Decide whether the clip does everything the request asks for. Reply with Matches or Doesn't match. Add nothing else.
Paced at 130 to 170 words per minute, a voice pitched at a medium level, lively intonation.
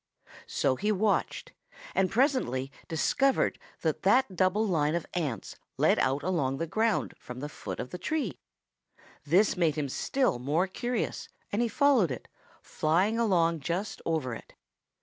Matches